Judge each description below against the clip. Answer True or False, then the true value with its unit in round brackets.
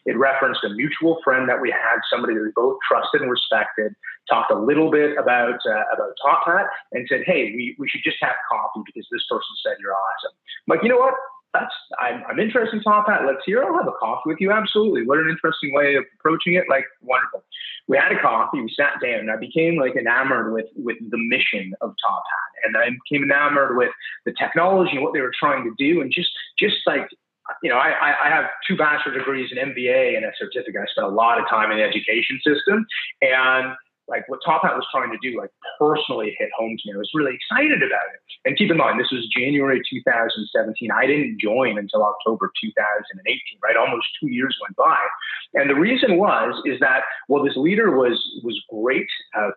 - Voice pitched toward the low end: False (150 Hz)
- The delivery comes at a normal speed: False (230 wpm)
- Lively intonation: True (8.5 semitones)